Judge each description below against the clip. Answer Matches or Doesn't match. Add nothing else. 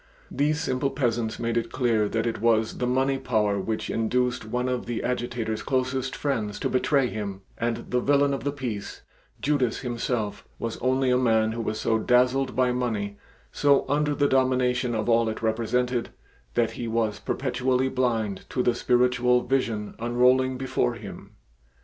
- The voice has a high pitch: Doesn't match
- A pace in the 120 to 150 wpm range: Doesn't match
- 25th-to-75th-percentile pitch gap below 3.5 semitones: Matches